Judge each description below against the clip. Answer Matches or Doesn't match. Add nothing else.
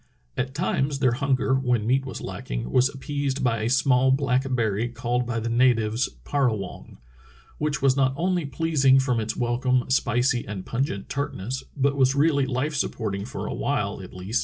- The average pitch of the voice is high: Doesn't match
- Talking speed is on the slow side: Doesn't match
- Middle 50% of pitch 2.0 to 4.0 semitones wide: Matches